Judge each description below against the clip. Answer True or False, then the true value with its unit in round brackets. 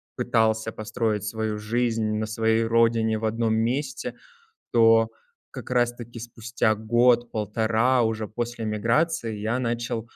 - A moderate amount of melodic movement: False (1.4 semitones)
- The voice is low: True (115 Hz)